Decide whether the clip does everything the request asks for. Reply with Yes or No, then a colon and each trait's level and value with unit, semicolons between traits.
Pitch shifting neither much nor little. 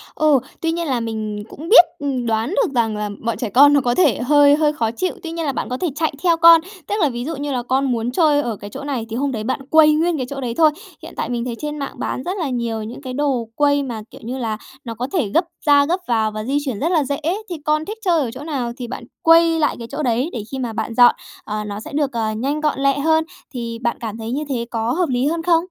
Yes: average, 4.7 semitones